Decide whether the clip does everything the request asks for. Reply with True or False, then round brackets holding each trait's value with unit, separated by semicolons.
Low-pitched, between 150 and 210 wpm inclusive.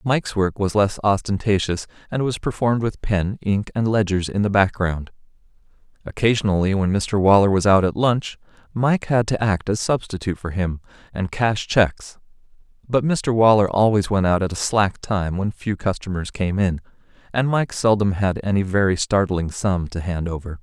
True (100 Hz; 175 wpm)